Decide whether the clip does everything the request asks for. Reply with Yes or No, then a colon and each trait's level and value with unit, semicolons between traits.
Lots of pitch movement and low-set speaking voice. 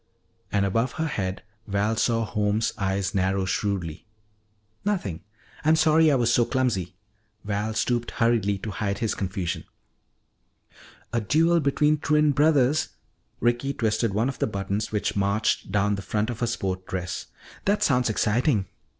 No: average, 4.6 semitones; low, 110 Hz